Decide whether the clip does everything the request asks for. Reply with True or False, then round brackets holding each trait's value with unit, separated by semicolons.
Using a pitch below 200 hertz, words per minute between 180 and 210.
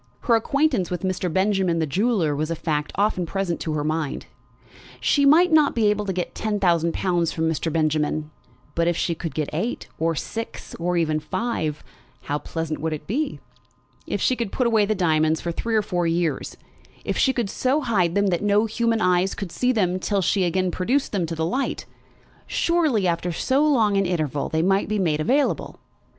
True (185 Hz; 205 wpm)